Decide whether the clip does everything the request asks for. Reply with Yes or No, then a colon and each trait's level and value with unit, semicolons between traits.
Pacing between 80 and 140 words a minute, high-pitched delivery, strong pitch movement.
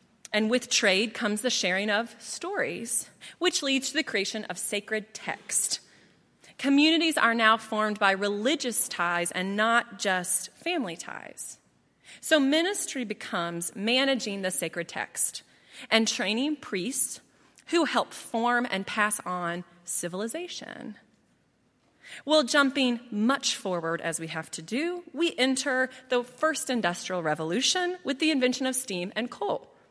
Yes: slow, 135 wpm; high, 230 Hz; wide, 5.7 semitones